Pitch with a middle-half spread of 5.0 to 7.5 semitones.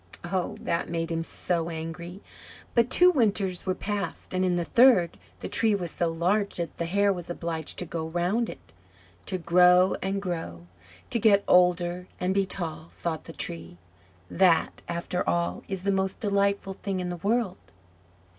No: average, 2.8 semitones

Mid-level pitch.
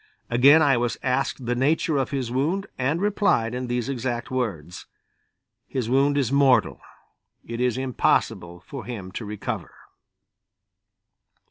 No: low, 125 Hz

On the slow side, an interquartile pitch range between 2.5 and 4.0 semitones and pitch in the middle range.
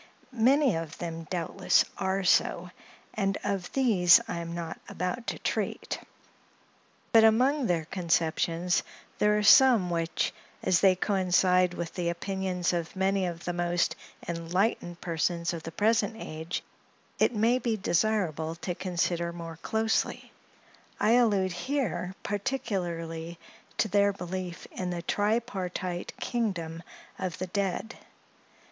Yes: slow, 130 wpm; average, 3.5 semitones; medium, 180 Hz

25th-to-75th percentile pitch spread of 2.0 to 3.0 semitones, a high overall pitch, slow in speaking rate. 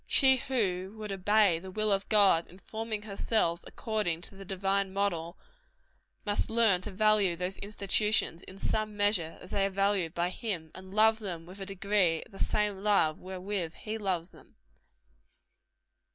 No: average, 2.7 semitones; high, 195 Hz; average, 165 wpm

